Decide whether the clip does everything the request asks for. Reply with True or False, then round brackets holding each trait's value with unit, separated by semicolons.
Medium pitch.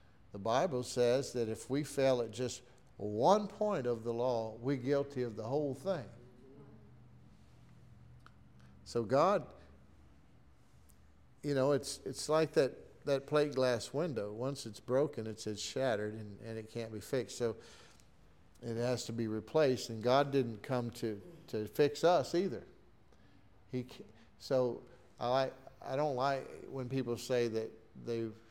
False (120 Hz)